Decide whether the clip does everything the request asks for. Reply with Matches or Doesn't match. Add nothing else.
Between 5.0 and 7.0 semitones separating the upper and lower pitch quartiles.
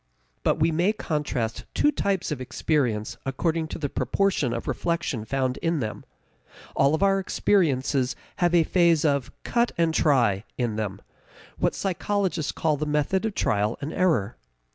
Matches